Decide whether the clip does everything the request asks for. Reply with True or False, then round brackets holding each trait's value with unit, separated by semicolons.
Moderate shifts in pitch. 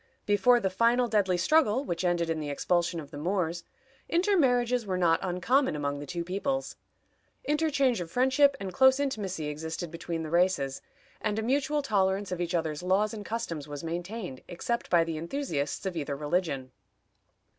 False (6.6 semitones)